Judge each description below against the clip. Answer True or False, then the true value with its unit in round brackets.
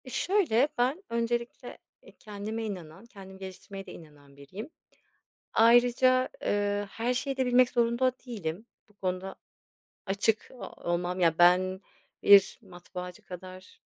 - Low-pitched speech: False (205 Hz)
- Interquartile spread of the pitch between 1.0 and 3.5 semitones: False (4.7 semitones)